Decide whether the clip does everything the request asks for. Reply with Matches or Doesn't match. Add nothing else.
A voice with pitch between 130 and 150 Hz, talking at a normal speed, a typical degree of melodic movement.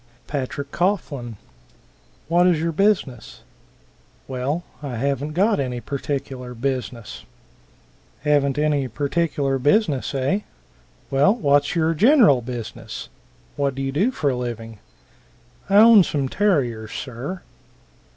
Doesn't match